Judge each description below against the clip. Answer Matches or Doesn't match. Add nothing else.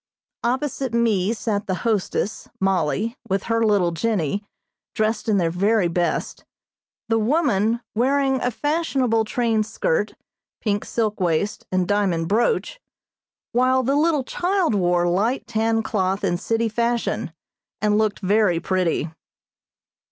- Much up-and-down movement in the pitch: Doesn't match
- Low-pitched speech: Doesn't match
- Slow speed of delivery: Matches